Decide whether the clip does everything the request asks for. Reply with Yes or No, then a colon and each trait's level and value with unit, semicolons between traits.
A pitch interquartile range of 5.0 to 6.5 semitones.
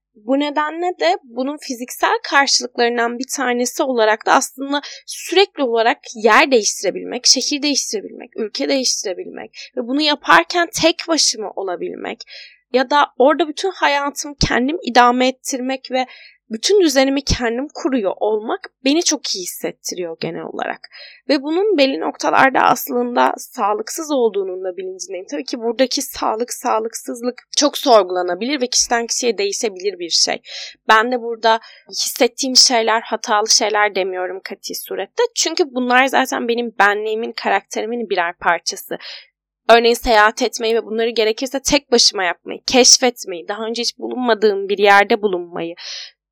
No: average, 4.5 semitones